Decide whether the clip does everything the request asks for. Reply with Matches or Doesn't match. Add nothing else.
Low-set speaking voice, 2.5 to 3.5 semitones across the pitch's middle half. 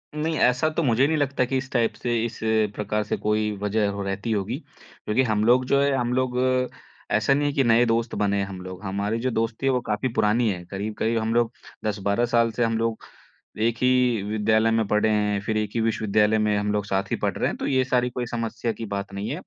Matches